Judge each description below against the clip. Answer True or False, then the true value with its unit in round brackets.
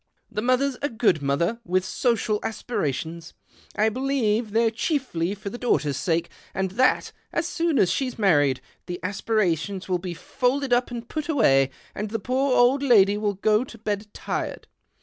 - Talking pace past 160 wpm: True (170 wpm)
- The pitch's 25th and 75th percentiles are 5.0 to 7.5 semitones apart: True (5.4 semitones)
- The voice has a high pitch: True (215 Hz)